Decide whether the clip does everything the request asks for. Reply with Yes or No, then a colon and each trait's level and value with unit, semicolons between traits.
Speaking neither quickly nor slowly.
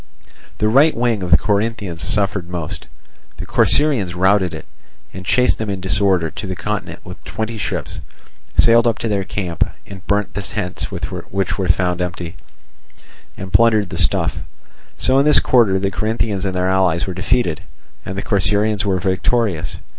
Yes: average, 170 wpm